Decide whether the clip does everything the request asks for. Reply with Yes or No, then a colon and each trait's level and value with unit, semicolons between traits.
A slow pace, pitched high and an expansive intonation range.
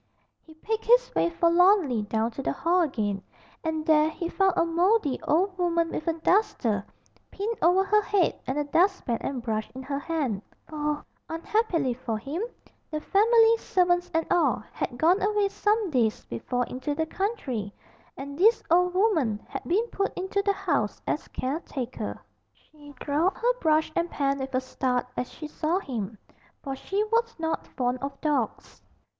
No: average, 170 wpm; very high, 320 Hz; wide, 6.4 semitones